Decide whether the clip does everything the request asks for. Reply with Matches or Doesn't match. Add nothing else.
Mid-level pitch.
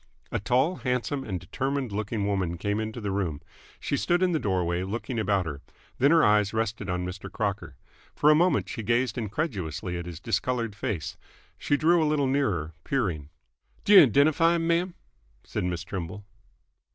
Doesn't match